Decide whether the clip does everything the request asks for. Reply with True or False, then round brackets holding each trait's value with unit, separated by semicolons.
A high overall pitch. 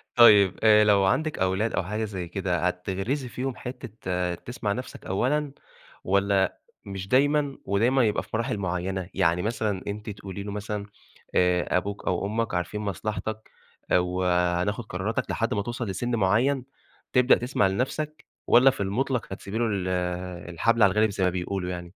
False (100 Hz)